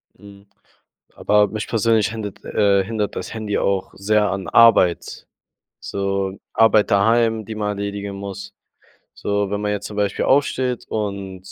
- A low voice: Yes, low, 105 Hz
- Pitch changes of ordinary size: No, narrow, 1.7 semitones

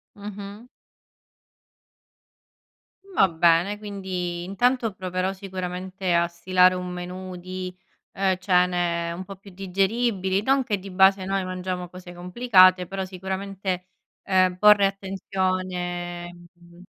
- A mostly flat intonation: Yes, narrow, 1.5 semitones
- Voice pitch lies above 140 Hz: Yes, medium, 185 Hz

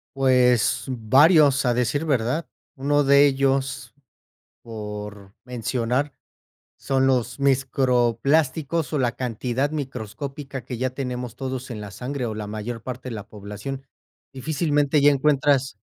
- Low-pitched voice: Yes, low, 130 Hz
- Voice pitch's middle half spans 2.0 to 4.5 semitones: Yes, average, 2.8 semitones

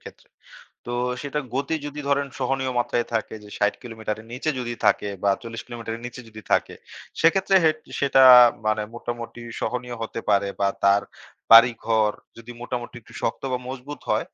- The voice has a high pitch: No, low, 120 Hz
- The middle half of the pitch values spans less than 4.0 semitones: Yes, average, 3.0 semitones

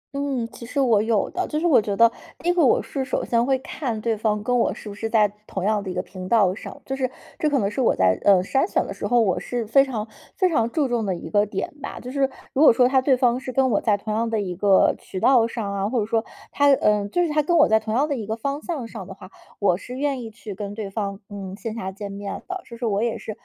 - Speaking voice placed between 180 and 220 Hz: No, high, 230 Hz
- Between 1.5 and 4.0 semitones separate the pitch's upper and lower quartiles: No, average, 4.5 semitones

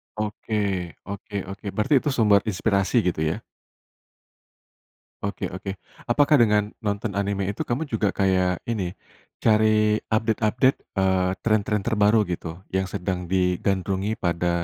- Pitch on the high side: No, low, 100 Hz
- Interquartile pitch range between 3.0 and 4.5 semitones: No, narrow, 2.4 semitones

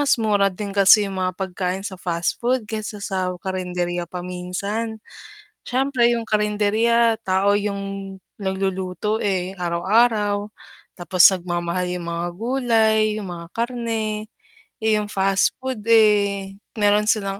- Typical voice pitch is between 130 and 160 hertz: No, high, 200 Hz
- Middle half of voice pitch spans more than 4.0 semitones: No, average, 2.9 semitones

